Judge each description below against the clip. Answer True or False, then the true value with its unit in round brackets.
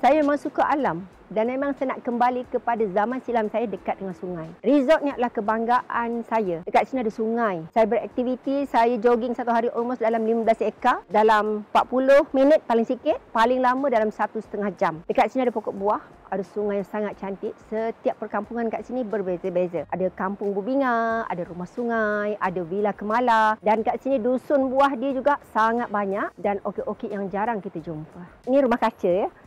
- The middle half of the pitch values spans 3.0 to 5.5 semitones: True (3.3 semitones)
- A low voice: False (225 Hz)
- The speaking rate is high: True (185 wpm)